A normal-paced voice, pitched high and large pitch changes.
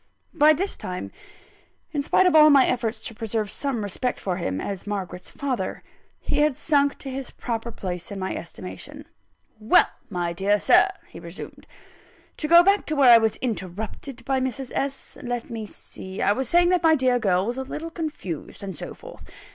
Yes: average, 190 wpm; high, 245 Hz; wide, 6.0 semitones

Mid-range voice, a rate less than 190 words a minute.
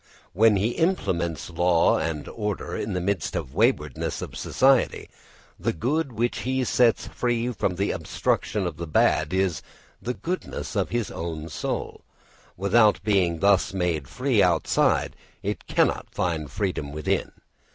No: very low, 95 Hz; average, 150 wpm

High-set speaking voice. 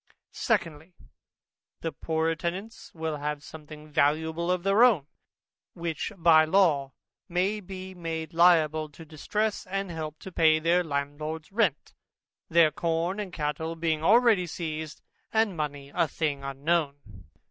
No: medium, 165 Hz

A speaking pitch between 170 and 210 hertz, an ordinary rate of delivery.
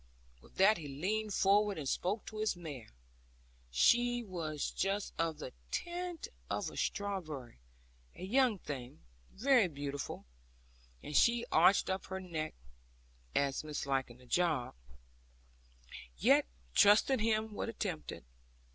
No: medium, 185 Hz; slow, 130 wpm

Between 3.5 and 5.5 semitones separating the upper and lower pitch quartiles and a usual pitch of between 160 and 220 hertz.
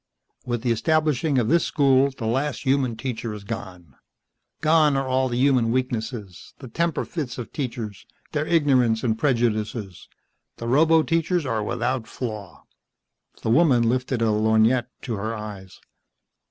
No: average, 3.8 semitones; low, 120 Hz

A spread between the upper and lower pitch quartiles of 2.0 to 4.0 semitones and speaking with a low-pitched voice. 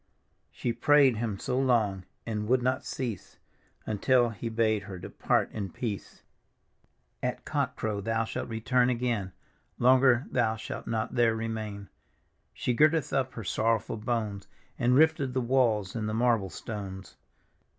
Yes: average, 2.9 semitones; low, 115 Hz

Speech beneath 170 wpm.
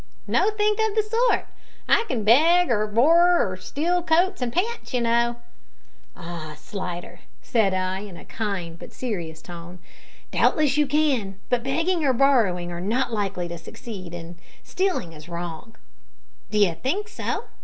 Yes: average, 155 wpm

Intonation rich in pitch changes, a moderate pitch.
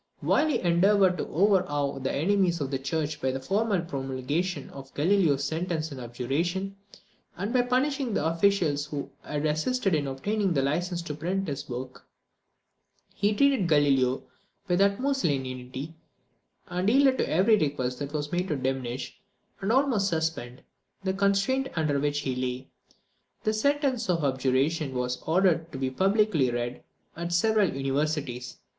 Yes: wide, 6.3 semitones; medium, 160 Hz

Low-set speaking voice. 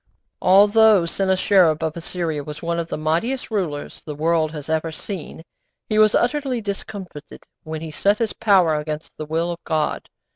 No: medium, 170 Hz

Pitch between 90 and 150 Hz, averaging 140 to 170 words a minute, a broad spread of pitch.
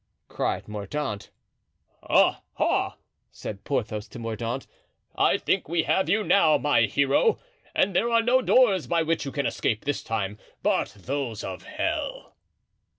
Yes: medium, 140 Hz; average, 150 wpm; wide, 7.7 semitones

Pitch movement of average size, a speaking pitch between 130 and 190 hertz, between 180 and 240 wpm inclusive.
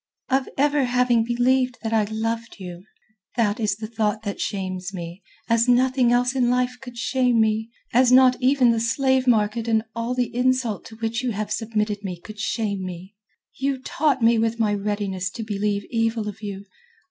No: average, 3.1 semitones; high, 225 Hz; average, 190 wpm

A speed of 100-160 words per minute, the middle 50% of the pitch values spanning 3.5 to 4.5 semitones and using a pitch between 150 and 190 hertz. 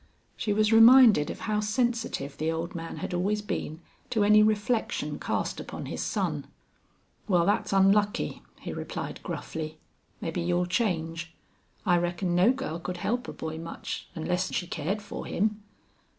Yes: average, 155 wpm; average, 4.1 semitones; medium, 185 Hz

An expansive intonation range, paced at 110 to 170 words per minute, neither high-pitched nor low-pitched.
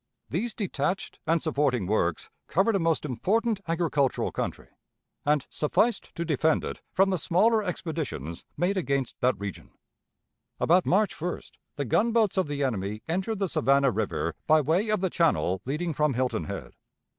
Yes: wide, 5.9 semitones; average, 155 wpm; medium, 160 Hz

